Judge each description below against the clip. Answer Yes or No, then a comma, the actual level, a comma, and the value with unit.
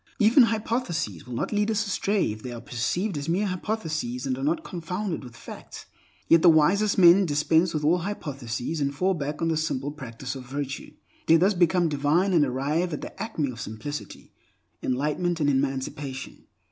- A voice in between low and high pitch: Yes, medium, 155 Hz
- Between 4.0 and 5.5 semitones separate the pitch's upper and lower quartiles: Yes, average, 5.2 semitones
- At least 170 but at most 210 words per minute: Yes, average, 185 wpm